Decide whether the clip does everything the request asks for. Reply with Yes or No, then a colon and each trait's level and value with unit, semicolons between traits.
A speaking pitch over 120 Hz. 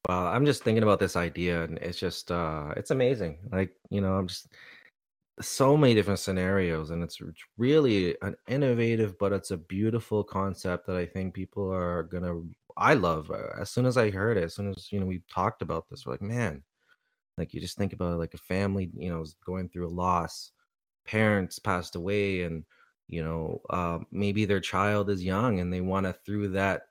No: very low, 95 Hz